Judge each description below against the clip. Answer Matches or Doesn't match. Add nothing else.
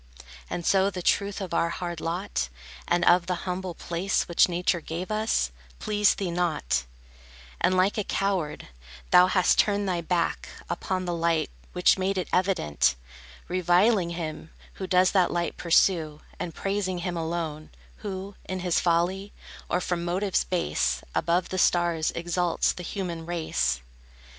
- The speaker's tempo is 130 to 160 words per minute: Matches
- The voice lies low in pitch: Doesn't match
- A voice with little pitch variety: Matches